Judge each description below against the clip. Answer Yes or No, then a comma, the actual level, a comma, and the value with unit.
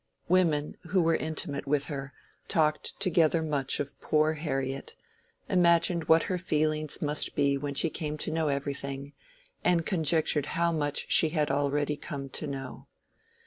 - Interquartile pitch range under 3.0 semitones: Yes, narrow, 2.6 semitones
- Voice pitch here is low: No, medium, 150 Hz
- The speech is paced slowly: No, average, 150 wpm